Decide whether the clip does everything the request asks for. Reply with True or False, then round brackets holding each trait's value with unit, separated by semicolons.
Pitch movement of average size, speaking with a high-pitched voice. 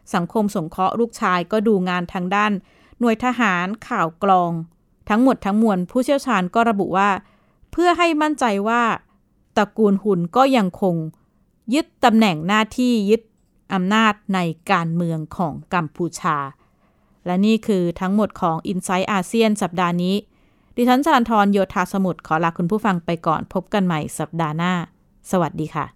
True (3.9 semitones; 195 Hz)